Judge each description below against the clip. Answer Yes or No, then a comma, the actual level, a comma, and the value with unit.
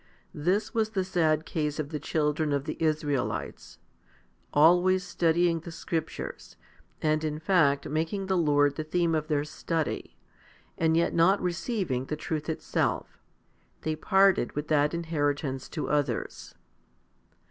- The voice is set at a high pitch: No, medium, 155 Hz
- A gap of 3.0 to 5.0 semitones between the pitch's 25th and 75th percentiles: No, narrow, 2.6 semitones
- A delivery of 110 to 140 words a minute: Yes, slow, 135 wpm